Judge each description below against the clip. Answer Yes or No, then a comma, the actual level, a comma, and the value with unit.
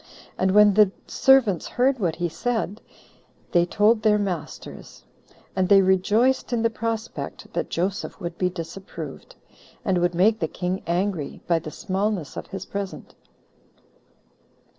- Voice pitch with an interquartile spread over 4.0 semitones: No, average, 3.4 semitones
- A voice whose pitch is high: Yes, high, 195 Hz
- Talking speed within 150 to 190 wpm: No, average, 140 wpm